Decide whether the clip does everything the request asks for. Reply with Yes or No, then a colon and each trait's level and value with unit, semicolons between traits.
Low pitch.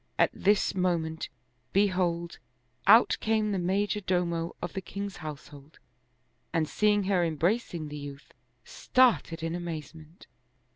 No: medium, 175 Hz